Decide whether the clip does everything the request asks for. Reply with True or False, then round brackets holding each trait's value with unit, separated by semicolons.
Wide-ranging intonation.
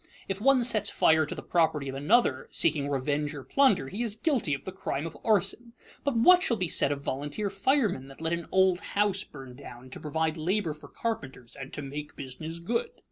True (6.8 semitones)